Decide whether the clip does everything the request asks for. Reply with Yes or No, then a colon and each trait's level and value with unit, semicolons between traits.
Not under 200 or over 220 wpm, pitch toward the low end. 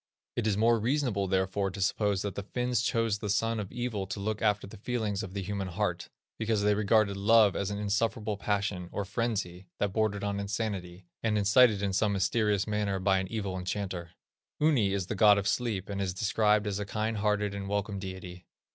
Yes: fast, 205 wpm; low, 100 Hz